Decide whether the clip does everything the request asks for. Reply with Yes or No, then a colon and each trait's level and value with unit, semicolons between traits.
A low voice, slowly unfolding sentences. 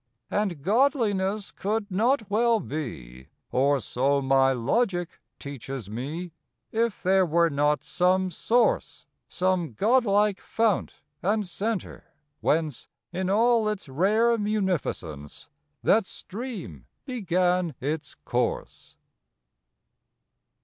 No: medium, 185 Hz; slow, 100 wpm